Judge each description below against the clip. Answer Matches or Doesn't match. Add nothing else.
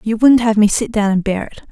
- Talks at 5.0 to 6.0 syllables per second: Matches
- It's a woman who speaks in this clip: Matches